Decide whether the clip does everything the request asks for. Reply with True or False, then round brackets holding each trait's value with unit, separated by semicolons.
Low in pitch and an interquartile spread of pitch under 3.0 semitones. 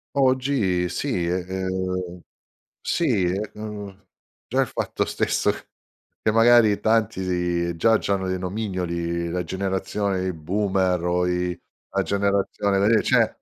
True (95 Hz; 2.6 semitones)